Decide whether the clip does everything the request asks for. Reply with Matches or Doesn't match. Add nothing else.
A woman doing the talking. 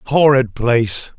Doesn't match